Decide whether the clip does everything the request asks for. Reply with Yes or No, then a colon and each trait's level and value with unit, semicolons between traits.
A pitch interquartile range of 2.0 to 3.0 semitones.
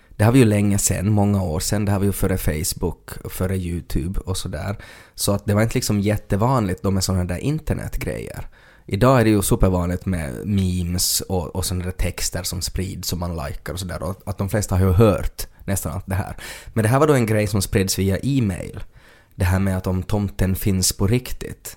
Yes: narrow, 2.6 semitones